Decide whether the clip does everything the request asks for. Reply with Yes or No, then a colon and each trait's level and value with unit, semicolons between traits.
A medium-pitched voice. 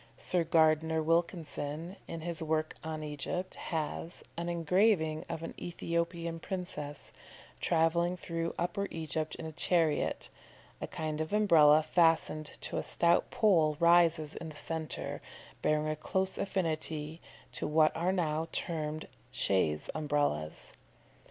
Yes: medium, 160 Hz